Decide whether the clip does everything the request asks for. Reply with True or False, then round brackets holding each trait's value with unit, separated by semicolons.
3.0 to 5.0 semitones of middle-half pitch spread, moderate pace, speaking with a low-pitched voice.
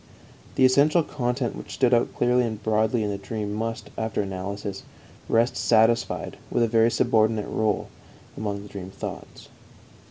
False (2.6 semitones; 155 wpm; 110 Hz)